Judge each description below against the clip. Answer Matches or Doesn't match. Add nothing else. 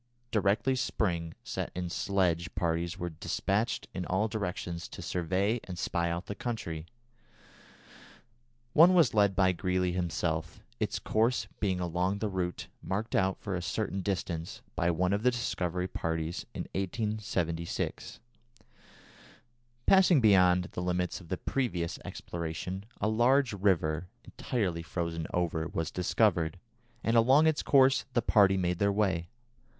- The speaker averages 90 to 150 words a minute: Matches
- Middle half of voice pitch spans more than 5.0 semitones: Doesn't match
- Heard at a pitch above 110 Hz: Doesn't match